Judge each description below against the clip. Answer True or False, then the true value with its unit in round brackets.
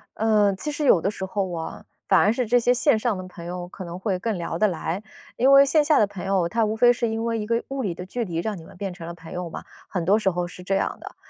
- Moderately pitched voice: False (200 Hz)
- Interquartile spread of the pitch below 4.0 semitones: False (4.4 semitones)